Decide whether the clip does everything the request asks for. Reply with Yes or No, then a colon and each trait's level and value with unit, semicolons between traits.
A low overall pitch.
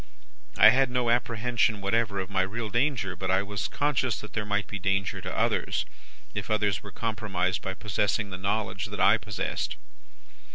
Yes: low, 105 Hz